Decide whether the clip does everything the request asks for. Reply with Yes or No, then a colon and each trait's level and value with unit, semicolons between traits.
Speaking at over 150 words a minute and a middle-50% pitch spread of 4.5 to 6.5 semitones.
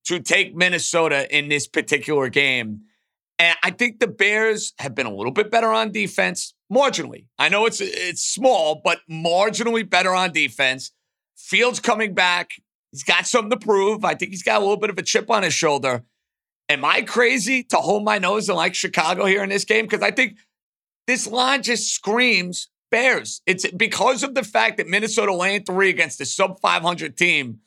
Yes: average, 190 wpm; average, 4.9 semitones